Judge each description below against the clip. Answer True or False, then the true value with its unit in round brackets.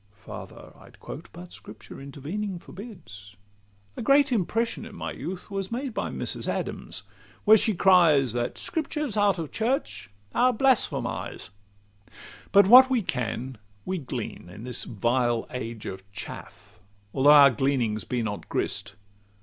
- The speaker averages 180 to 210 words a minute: False (145 wpm)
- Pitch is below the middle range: False (145 Hz)